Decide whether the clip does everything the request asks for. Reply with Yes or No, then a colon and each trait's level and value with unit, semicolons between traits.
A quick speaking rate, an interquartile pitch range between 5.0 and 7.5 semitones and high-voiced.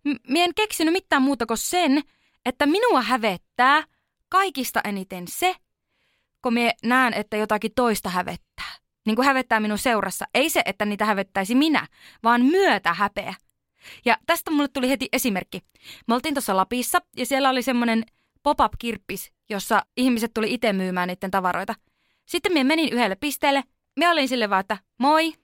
Yes: fast, 160 wpm; average, 5.3 semitones; very high, 250 Hz